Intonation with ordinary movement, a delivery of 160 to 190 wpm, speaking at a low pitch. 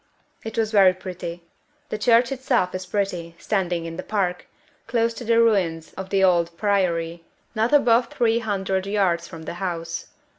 No: average, 4.2 semitones; average, 170 wpm; high, 190 Hz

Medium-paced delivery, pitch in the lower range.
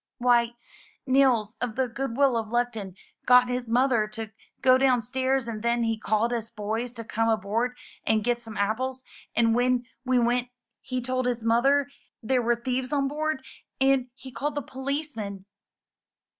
No: average, 165 wpm; high, 245 Hz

